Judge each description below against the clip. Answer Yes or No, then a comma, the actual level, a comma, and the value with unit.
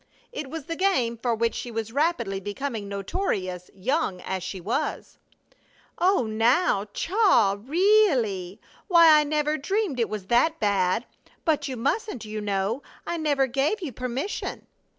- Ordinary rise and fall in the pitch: No, wide, 7.7 semitones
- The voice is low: No, very high, 250 Hz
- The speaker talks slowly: No, average, 150 wpm